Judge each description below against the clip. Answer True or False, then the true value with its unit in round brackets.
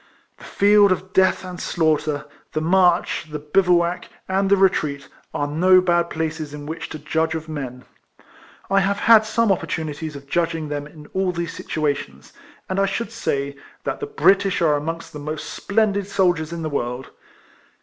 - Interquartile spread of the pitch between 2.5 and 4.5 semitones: True (4.1 semitones)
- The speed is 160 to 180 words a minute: True (170 wpm)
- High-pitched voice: False (165 Hz)